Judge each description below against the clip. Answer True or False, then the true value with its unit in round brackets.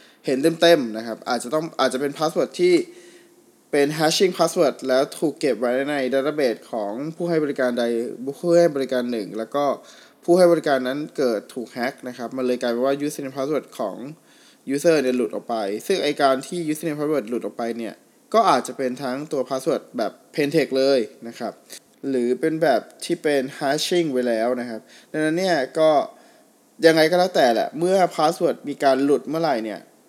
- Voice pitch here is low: False (145 Hz)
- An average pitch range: True (4.8 semitones)